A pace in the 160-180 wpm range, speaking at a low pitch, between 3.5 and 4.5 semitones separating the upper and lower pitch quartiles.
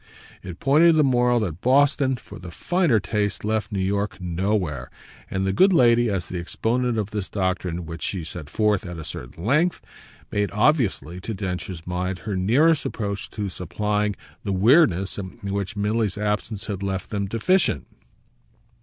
Yes: average, 165 wpm; low, 100 Hz; average, 4.2 semitones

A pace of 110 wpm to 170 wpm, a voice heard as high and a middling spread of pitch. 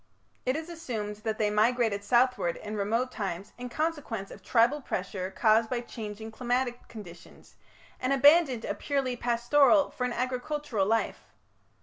Yes: average, 145 wpm; high, 240 Hz; average, 3.5 semitones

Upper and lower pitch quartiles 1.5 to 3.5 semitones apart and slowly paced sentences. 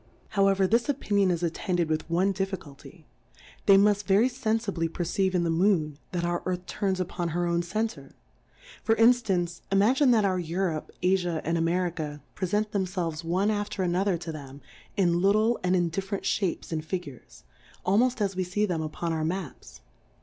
No: average, 3.0 semitones; average, 185 wpm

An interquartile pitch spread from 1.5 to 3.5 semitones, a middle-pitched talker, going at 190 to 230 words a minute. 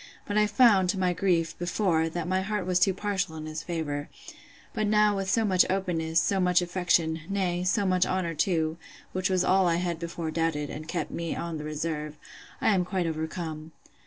Yes: average, 2.7 semitones; medium, 175 Hz; average, 200 wpm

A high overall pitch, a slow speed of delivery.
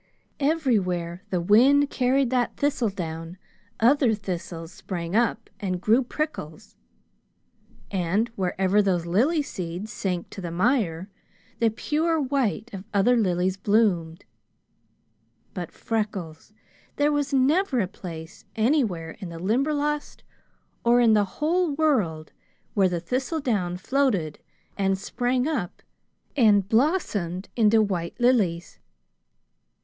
Yes: high, 210 Hz; slow, 115 wpm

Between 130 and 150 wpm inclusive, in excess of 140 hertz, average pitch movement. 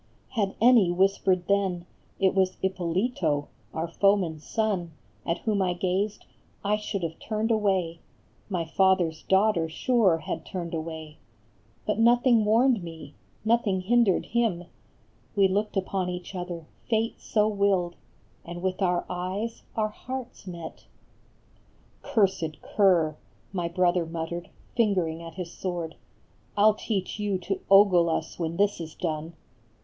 Yes: average, 145 wpm; medium, 185 Hz; average, 3.6 semitones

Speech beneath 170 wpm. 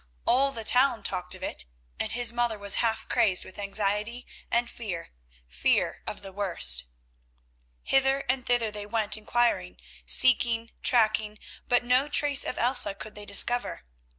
Yes: average, 150 wpm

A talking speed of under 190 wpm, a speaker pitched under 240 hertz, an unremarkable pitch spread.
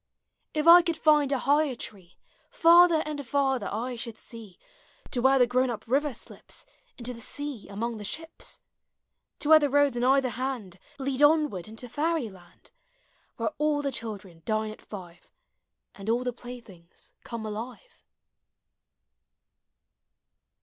No: average, 150 wpm; very high, 250 Hz; average, 4.9 semitones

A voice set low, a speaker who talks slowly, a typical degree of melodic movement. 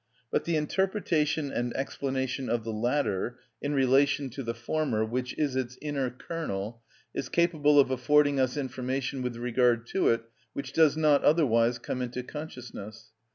No: low, 130 Hz; average, 155 wpm; average, 3.6 semitones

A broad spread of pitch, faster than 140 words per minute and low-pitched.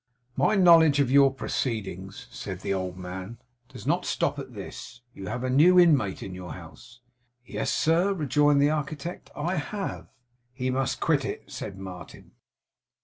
Yes: wide, 8.0 semitones; average, 160 wpm; low, 130 Hz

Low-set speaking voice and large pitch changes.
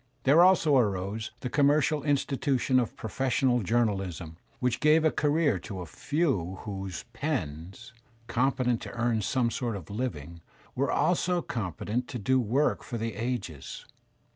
Yes: low, 120 Hz; wide, 5.9 semitones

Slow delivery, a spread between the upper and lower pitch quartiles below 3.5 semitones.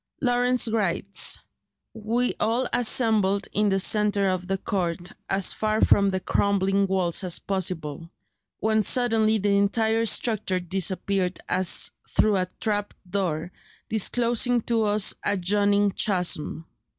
Yes: slow, 125 wpm; average, 2.7 semitones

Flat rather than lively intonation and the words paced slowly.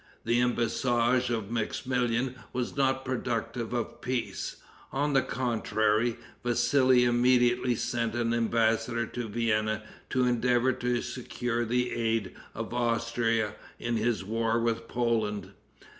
Yes: narrow, 1.4 semitones; slow, 120 wpm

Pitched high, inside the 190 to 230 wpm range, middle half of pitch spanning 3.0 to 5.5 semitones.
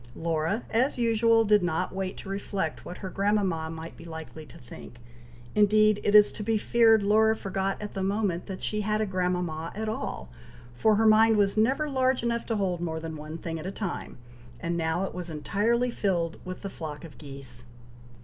Yes: high, 195 Hz; average, 200 wpm; average, 4.6 semitones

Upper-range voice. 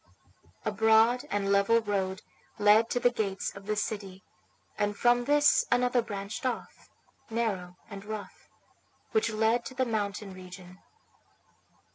Yes: high, 215 Hz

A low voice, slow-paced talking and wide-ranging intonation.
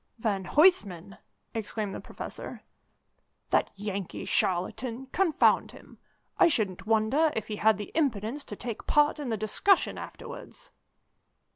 No: high, 220 Hz; slow, 130 wpm; wide, 6.1 semitones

